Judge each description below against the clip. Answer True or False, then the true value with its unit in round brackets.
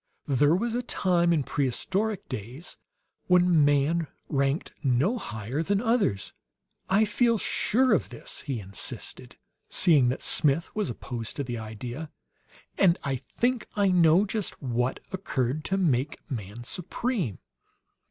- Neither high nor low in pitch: True (155 Hz)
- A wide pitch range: True (7.4 semitones)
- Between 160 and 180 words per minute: False (135 wpm)